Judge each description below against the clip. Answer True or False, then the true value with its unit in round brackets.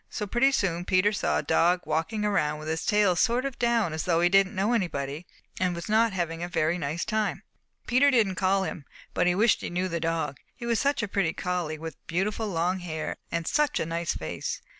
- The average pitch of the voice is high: False (180 Hz)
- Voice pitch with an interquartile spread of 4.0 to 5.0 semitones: True (4.4 semitones)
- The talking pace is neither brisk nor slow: False (225 wpm)